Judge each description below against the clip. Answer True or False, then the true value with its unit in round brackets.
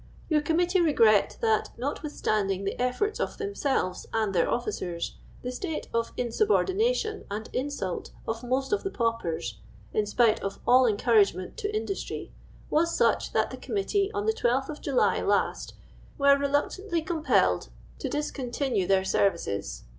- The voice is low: False (255 Hz)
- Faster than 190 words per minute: False (145 wpm)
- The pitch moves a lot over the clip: True (7.9 semitones)